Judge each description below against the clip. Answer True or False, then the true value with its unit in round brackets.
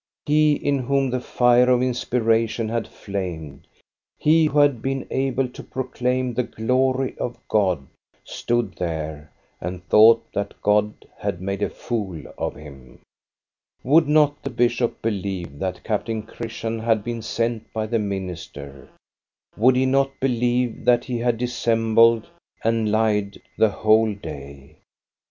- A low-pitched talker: True (115 Hz)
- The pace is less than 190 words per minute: True (140 wpm)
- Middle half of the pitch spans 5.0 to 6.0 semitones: False (3.8 semitones)